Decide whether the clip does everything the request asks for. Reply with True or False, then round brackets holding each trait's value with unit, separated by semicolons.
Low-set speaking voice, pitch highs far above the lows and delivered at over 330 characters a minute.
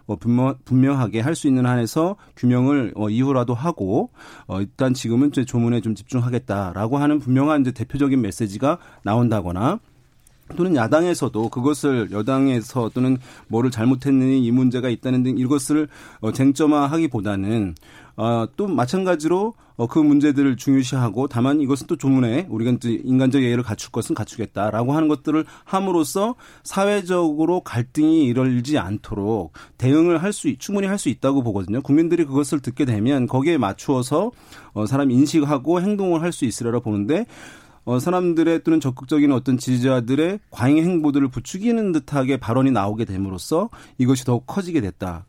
False (130 Hz; 4.4 semitones; 360 characters per minute)